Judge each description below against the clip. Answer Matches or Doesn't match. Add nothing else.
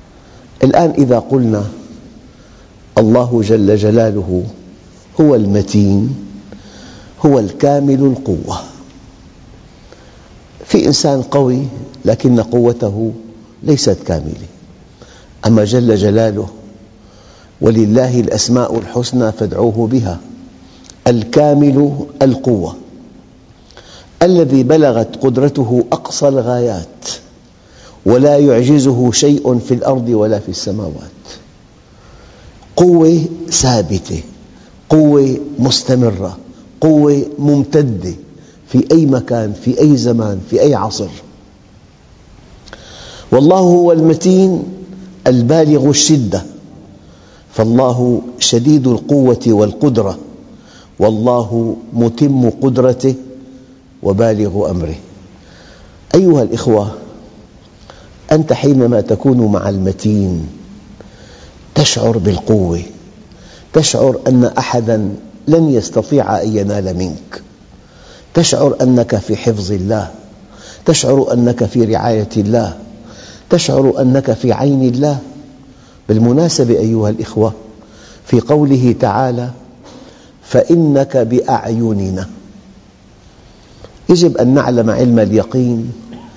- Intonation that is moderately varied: Matches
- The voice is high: Doesn't match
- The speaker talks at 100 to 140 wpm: Doesn't match